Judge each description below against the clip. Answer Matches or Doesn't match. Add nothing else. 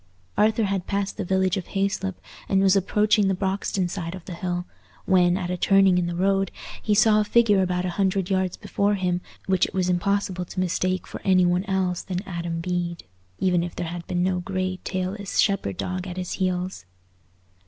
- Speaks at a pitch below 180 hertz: Doesn't match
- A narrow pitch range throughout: Matches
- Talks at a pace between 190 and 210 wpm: Matches